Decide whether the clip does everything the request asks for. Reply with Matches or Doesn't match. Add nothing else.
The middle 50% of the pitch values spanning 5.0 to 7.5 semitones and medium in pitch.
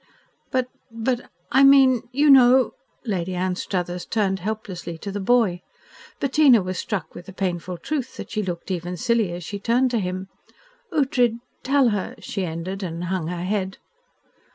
Doesn't match